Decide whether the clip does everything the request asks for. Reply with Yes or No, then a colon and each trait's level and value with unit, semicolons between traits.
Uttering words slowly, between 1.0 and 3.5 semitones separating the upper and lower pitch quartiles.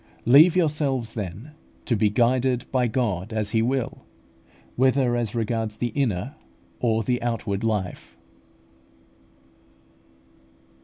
Yes: slow, 110 wpm; average, 3.1 semitones